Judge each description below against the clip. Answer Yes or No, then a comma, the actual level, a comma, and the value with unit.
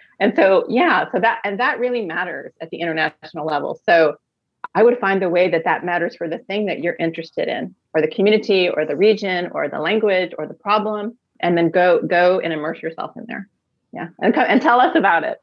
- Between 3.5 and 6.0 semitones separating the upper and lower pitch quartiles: Yes, average, 3.9 semitones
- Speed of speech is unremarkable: No, fast, 220 wpm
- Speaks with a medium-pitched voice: Yes, medium, 180 Hz